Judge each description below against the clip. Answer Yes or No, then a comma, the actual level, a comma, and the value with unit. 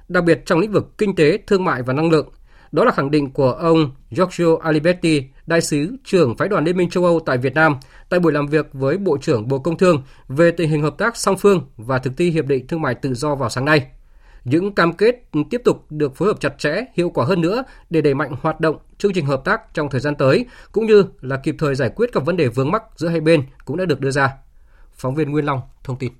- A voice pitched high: No, medium, 155 Hz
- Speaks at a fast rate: Yes, fast, 260 wpm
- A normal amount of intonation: Yes, average, 4.3 semitones